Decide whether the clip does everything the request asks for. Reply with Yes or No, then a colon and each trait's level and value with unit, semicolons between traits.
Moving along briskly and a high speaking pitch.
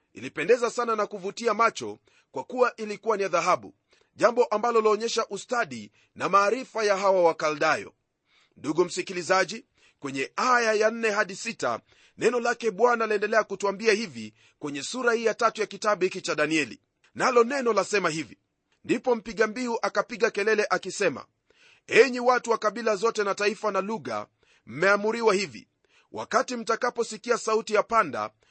Yes: fast, 145 wpm; high, 220 Hz